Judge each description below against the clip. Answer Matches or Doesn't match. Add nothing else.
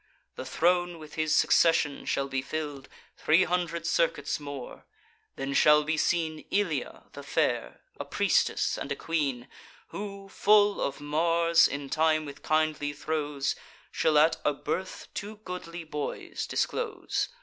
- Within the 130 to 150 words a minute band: Matches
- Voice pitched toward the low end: Doesn't match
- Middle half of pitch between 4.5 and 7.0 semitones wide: Doesn't match